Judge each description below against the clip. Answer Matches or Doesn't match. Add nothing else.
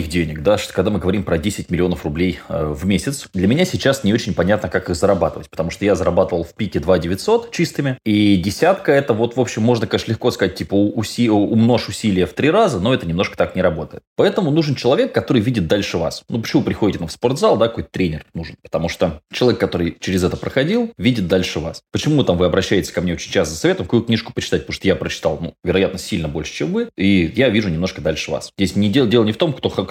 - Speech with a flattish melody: Doesn't match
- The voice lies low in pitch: Matches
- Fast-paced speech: Matches